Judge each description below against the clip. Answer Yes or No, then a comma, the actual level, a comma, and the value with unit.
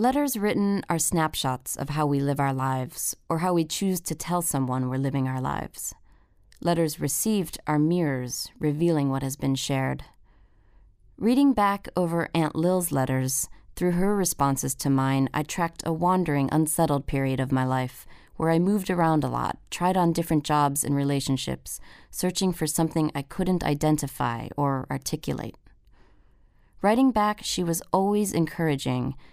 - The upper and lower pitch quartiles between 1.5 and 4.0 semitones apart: No, average, 4.7 semitones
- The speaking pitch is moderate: Yes, medium, 150 Hz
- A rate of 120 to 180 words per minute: Yes, average, 155 wpm